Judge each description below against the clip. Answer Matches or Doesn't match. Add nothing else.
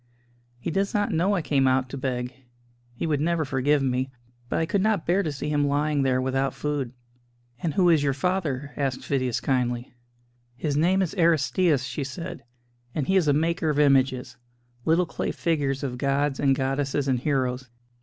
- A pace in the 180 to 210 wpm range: Matches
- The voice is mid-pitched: Matches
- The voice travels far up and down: Doesn't match